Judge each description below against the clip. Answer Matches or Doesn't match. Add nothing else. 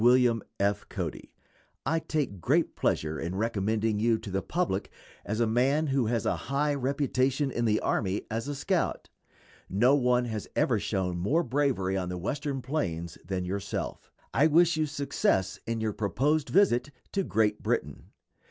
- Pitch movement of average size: Doesn't match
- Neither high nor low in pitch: Doesn't match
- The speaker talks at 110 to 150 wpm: Doesn't match